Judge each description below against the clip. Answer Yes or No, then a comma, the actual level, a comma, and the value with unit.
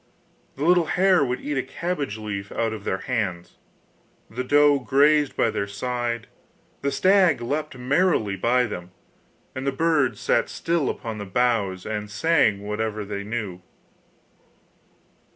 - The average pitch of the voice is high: No, low, 125 Hz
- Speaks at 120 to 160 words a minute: Yes, average, 145 wpm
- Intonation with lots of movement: Yes, wide, 5.8 semitones